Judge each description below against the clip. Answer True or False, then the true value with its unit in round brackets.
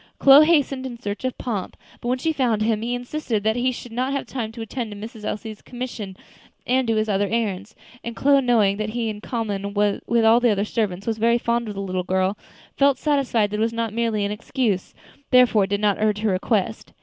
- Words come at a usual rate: False (225 wpm)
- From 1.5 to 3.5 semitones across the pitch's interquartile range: True (3.0 semitones)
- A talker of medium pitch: False (225 Hz)